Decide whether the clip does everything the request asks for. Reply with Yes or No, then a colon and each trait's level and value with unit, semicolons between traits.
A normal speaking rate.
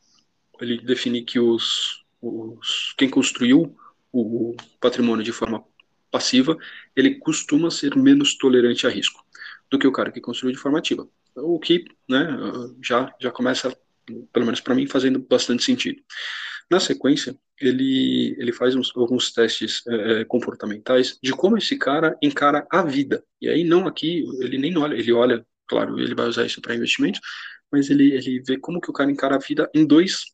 Yes: average, 170 wpm